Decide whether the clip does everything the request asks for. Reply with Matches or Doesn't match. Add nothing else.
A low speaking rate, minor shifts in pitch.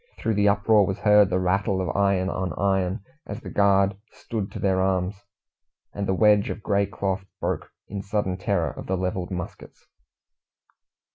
Doesn't match